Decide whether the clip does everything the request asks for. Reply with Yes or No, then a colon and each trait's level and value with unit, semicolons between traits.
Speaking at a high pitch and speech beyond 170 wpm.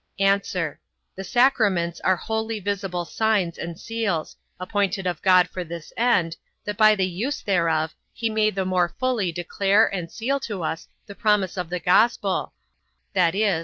No: high, 195 Hz; average, 160 wpm